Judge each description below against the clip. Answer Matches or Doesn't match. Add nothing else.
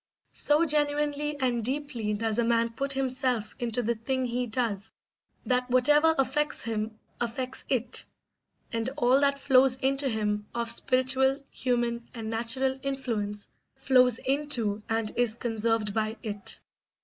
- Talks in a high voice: Matches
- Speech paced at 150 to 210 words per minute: Doesn't match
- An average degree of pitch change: Matches